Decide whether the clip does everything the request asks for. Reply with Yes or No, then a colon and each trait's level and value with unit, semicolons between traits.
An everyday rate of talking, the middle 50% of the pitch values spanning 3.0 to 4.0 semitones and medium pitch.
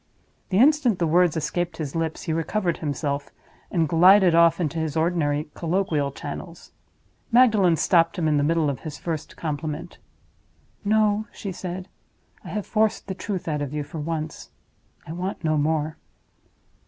Yes: average, 160 wpm; average, 3.3 semitones; medium, 165 Hz